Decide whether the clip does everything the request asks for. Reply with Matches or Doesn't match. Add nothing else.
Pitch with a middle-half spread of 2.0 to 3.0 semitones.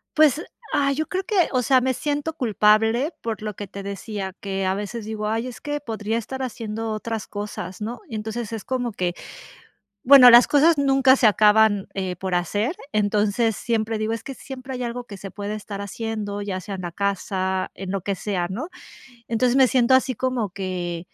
Doesn't match